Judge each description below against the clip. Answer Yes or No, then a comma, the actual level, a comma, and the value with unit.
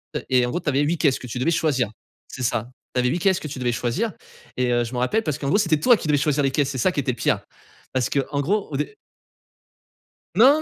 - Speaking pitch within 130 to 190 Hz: Yes, medium, 140 Hz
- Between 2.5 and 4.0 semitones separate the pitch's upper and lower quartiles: No, average, 4.8 semitones